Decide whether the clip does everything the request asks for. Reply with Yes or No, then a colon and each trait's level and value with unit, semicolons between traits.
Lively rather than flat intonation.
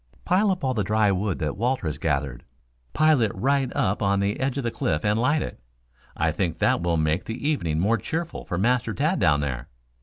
Yes: wide, 8.3 semitones